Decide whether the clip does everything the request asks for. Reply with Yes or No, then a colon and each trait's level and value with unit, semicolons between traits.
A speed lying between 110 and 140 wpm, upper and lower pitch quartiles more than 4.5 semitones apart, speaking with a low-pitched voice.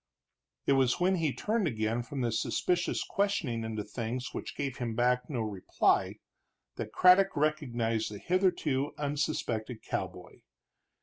Yes: slow, 135 wpm; wide, 5.5 semitones; low, 130 Hz